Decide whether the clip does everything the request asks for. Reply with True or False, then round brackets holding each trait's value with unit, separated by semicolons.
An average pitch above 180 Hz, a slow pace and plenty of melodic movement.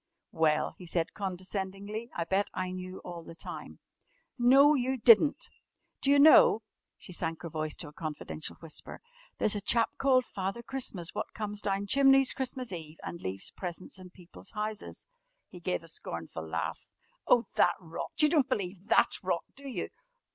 False (190 Hz; 170 wpm; 6.2 semitones)